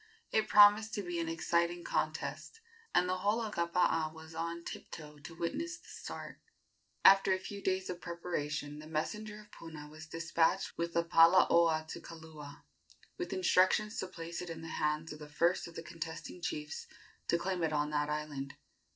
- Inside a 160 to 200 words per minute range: Yes, average, 180 wpm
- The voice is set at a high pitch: No, medium, 170 Hz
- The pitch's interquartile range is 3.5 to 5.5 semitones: No, average, 2.9 semitones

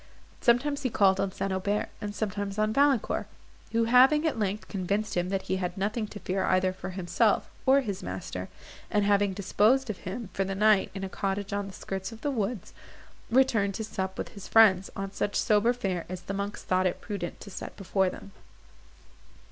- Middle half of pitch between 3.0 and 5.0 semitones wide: No, narrow, 2.6 semitones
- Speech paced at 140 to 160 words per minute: No, average, 200 wpm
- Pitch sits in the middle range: No, high, 200 Hz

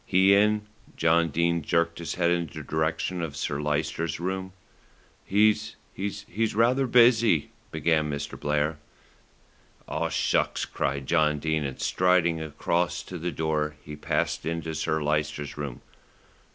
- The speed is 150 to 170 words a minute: No, average, 140 wpm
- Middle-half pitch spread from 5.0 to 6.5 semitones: No, average, 3.5 semitones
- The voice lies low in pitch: Yes, very low, 85 Hz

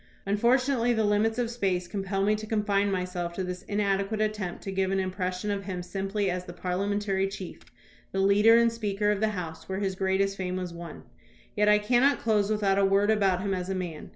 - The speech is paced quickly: Yes, fast, 215 wpm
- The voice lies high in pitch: Yes, high, 195 Hz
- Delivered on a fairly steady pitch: Yes, narrow, 2.1 semitones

